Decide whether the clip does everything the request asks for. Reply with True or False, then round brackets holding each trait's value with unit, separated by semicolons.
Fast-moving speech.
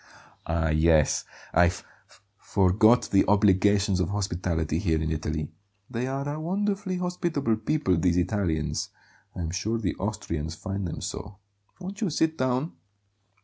False (140 wpm)